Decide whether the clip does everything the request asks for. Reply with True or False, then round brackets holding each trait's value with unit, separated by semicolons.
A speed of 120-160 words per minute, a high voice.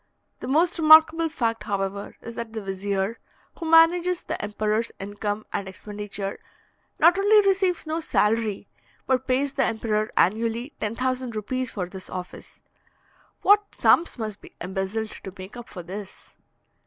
True (145 wpm; 225 Hz)